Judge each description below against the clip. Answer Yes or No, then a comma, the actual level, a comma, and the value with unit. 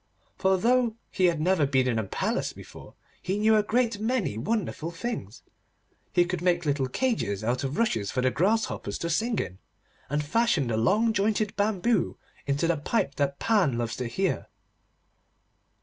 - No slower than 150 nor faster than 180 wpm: Yes, average, 170 wpm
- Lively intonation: Yes, wide, 8.4 semitones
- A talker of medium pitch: Yes, medium, 175 Hz